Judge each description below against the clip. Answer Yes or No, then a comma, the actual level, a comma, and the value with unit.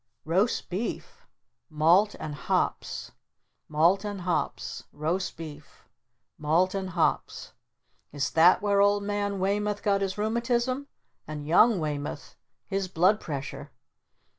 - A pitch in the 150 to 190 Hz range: Yes, medium, 185 Hz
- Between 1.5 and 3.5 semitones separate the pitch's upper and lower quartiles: No, average, 4.6 semitones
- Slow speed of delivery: Yes, slow, 115 wpm